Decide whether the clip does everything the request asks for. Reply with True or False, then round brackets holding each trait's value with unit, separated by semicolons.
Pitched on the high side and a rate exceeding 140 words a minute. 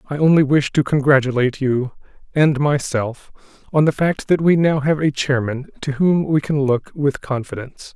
False (140 Hz; 180 wpm)